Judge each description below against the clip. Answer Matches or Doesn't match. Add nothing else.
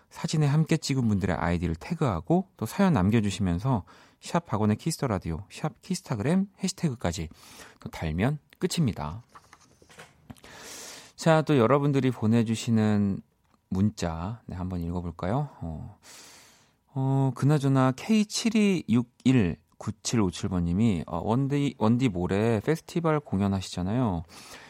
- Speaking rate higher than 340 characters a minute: Doesn't match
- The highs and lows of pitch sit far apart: Matches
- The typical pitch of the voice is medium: Doesn't match